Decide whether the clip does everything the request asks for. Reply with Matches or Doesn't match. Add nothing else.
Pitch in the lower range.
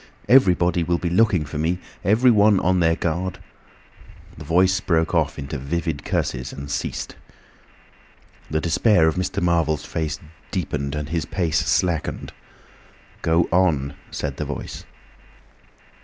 Matches